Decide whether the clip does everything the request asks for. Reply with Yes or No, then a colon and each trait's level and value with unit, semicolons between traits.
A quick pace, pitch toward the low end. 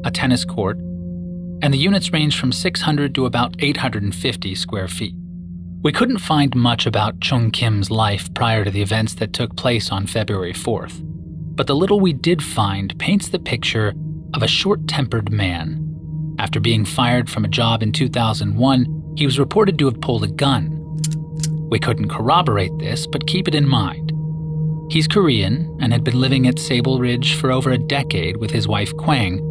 No: average, 175 wpm; low, 130 Hz